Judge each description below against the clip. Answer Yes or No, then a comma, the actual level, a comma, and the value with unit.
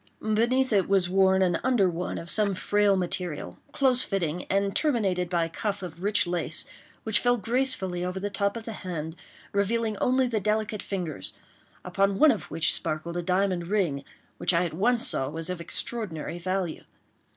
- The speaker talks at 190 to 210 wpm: No, average, 180 wpm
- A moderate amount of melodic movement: Yes, average, 3.5 semitones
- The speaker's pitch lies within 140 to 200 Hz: Yes, high, 190 Hz